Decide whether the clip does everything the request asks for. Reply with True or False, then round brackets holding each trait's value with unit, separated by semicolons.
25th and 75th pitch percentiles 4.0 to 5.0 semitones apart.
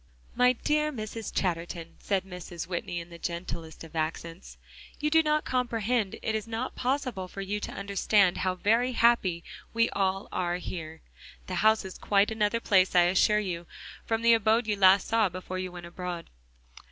True (4.3 semitones)